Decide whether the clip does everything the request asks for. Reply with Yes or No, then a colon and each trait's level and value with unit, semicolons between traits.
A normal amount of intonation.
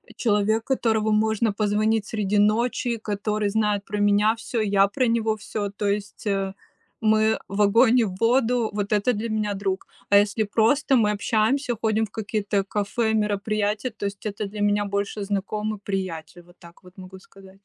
No: narrow, 1.6 semitones